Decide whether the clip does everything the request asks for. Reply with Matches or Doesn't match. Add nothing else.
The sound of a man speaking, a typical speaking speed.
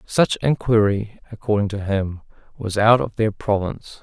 Matches